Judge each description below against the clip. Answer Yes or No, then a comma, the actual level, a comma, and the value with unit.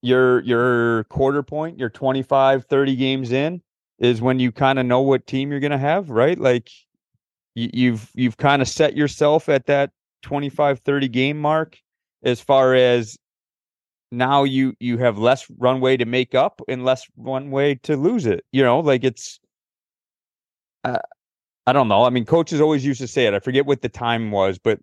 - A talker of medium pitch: No, low, 130 Hz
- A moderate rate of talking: Yes, average, 190 wpm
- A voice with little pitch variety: Yes, narrow, 2.2 semitones